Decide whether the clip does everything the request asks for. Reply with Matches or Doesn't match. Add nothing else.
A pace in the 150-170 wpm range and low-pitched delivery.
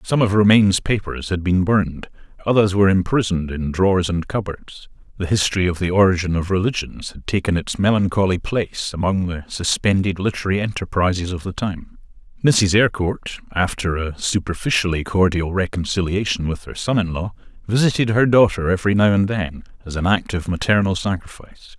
Matches